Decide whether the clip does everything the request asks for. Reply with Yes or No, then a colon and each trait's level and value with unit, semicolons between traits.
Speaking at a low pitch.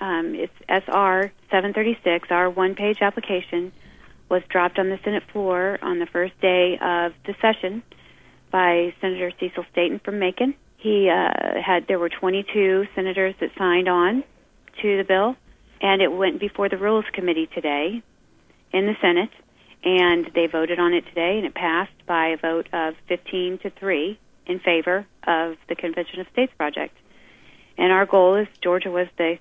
No: medium, 185 Hz